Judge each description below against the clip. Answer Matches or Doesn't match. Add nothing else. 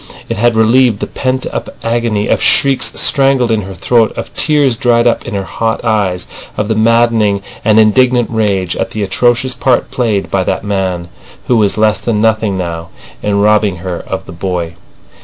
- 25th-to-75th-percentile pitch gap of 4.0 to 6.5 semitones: Doesn't match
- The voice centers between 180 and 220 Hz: Doesn't match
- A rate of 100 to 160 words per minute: Doesn't match